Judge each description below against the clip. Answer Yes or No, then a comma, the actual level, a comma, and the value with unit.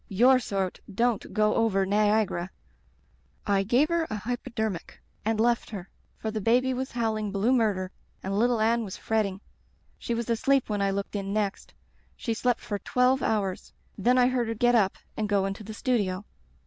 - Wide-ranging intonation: No, average, 3.3 semitones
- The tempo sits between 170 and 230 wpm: Yes, average, 180 wpm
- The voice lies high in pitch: Yes, high, 220 Hz